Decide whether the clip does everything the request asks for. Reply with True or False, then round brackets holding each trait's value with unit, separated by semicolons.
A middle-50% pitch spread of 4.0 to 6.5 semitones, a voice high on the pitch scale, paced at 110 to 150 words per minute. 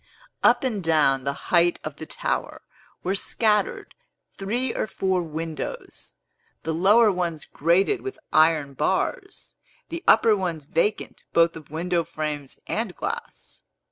False (5.0 semitones; 175 Hz; 135 wpm)